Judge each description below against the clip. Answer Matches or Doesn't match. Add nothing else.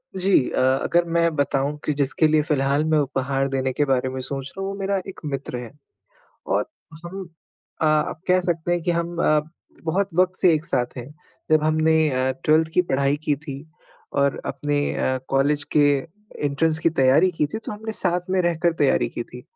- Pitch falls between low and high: Matches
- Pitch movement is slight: Doesn't match